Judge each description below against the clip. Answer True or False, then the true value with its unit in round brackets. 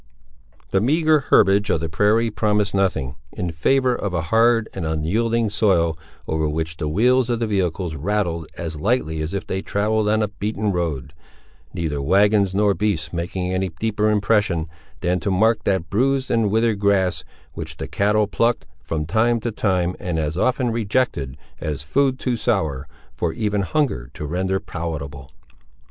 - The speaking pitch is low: True (100 Hz)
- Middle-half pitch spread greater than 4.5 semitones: True (5.1 semitones)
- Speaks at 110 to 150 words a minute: False (165 wpm)